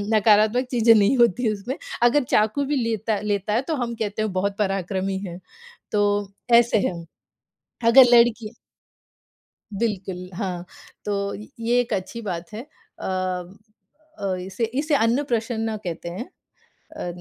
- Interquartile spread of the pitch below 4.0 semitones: Yes, average, 3.5 semitones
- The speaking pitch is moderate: No, high, 215 Hz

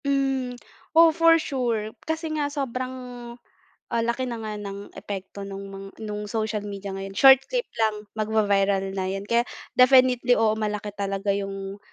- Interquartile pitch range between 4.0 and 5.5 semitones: Yes, average, 4.5 semitones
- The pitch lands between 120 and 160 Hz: No, high, 220 Hz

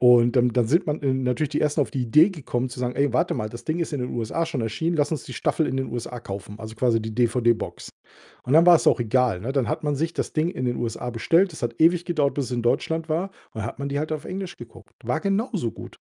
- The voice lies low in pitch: Yes, low, 130 Hz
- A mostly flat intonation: No, average, 5.0 semitones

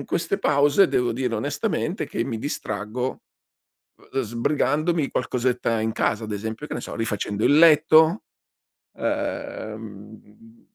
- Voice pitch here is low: Yes, low, 120 Hz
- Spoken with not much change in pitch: No, average, 5.1 semitones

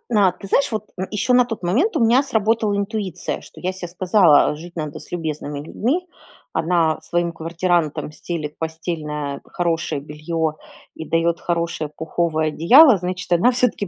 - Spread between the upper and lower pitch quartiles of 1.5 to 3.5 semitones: No, average, 4.6 semitones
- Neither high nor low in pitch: Yes, medium, 175 Hz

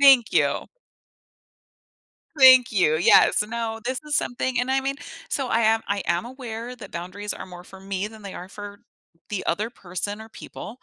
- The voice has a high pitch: Yes, high, 220 Hz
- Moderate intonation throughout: Yes, average, 4.2 semitones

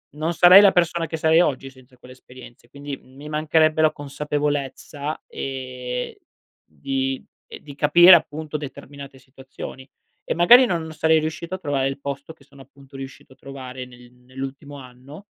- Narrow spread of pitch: No, average, 3.1 semitones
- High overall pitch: No, medium, 140 Hz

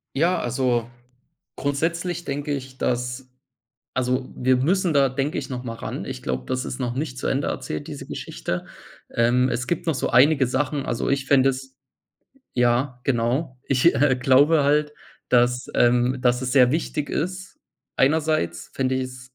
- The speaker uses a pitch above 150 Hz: No, low, 130 Hz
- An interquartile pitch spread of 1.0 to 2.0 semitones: No, average, 2.8 semitones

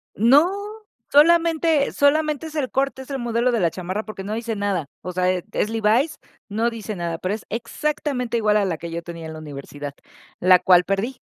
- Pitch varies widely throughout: Yes, wide, 6.9 semitones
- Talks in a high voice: Yes, high, 220 Hz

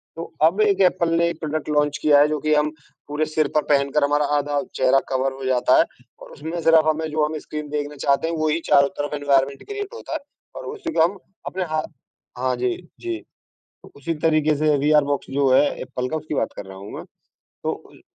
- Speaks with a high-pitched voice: No, medium, 150 Hz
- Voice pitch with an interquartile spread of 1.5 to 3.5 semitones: Yes, narrow, 2.4 semitones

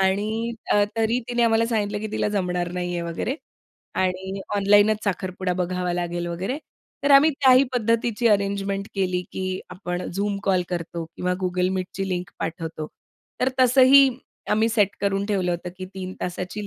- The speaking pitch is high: Yes, high, 195 Hz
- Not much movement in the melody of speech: No, average, 3.2 semitones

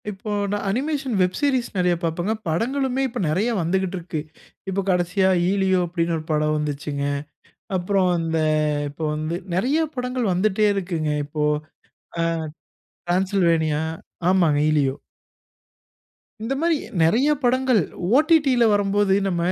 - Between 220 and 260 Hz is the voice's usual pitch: No, high, 190 Hz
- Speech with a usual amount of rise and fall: No, wide, 6.0 semitones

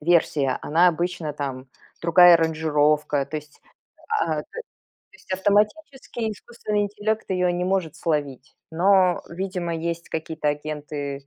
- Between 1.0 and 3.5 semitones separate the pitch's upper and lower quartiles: No, average, 4.0 semitones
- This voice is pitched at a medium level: Yes, medium, 165 Hz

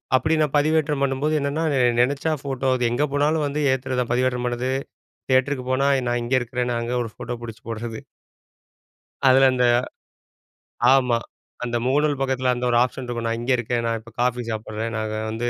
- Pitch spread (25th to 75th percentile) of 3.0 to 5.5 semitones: No, narrow, 2.5 semitones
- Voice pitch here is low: Yes, low, 125 Hz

